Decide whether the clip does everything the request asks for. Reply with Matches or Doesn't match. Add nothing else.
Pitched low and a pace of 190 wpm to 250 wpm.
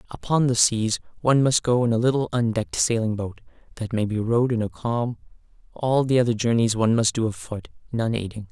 Matches